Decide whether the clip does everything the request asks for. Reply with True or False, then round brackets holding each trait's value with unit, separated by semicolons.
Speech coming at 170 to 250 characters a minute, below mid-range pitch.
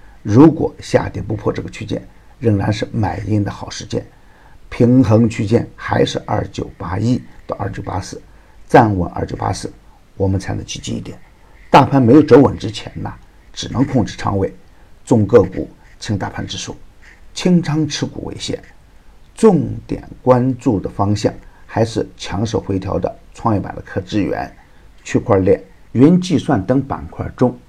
True (235 characters per minute; 115 Hz)